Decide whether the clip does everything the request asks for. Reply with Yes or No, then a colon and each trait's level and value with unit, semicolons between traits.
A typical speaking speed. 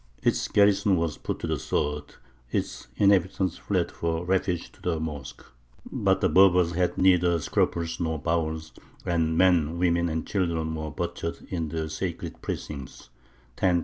Yes: average, 150 wpm